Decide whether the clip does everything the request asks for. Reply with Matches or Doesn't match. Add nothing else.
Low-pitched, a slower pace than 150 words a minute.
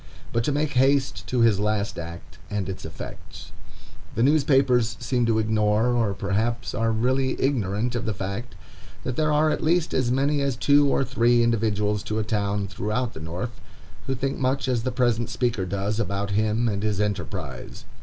Doesn't match